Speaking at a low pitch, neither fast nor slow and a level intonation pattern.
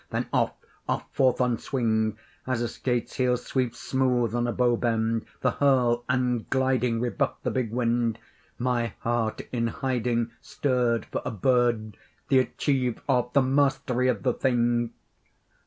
Yes: low, 120 Hz; average, 155 wpm; narrow, 1.6 semitones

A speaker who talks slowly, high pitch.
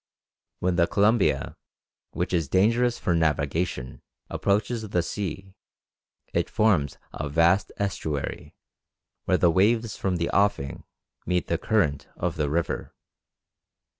No: slow, 120 wpm; very low, 90 Hz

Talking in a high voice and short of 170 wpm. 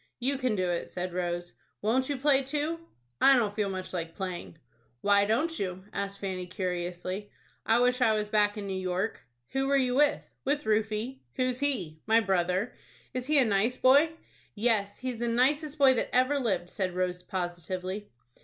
No: high, 215 Hz; average, 180 wpm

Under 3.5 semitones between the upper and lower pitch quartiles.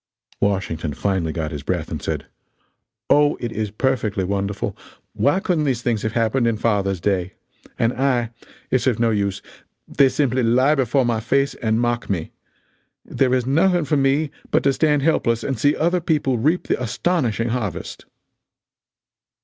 No: average, 4.8 semitones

